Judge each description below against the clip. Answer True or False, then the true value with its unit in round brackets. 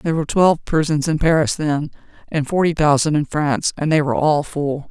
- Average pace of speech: False (210 wpm)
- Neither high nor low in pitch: True (150 Hz)